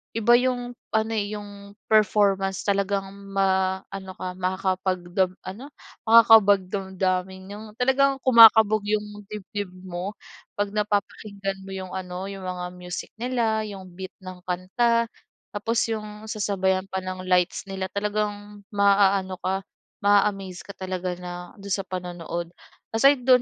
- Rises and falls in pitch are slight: Yes, narrow, 2.1 semitones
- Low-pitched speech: No, high, 195 Hz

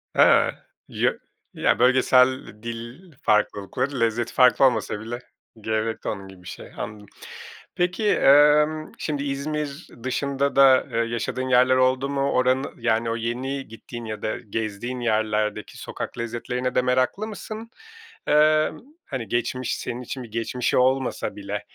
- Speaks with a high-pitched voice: No, low, 125 Hz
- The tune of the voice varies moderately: Yes, average, 3.3 semitones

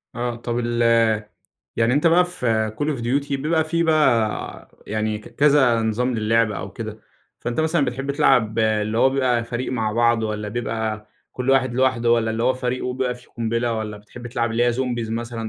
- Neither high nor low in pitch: No, low, 120 Hz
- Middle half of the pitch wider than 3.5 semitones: No, narrow, 2.6 semitones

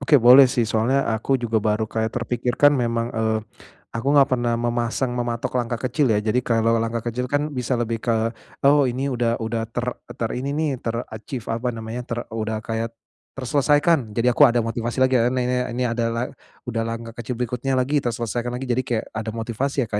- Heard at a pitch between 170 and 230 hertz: No, low, 120 Hz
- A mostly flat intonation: Yes, narrow, 1.8 semitones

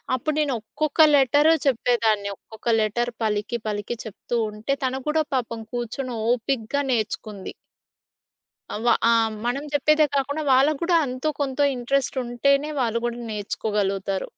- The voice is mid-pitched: No, high, 245 Hz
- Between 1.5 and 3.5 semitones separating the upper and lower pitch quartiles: No, average, 4.0 semitones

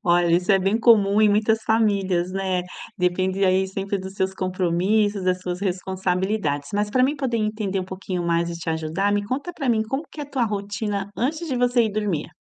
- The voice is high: Yes, high, 195 Hz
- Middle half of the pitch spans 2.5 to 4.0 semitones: Yes, average, 2.9 semitones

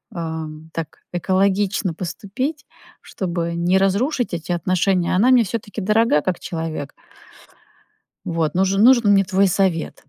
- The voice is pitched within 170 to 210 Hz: Yes, high, 190 Hz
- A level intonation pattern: No, average, 3.3 semitones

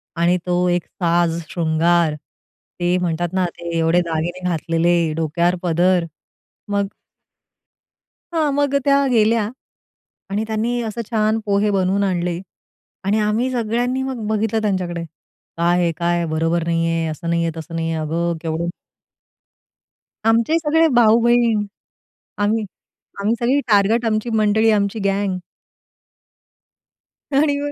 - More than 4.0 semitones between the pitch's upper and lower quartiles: Yes, average, 4.7 semitones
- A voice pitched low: No, medium, 185 Hz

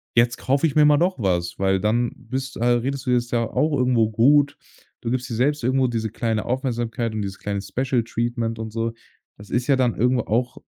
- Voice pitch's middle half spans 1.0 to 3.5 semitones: Yes, narrow, 2.6 semitones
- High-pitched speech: No, low, 120 Hz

